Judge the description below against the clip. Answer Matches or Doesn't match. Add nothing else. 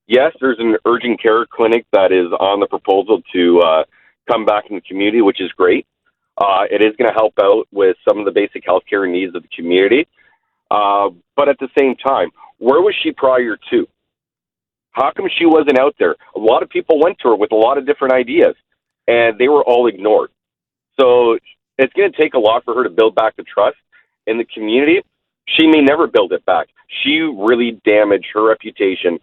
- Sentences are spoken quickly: Matches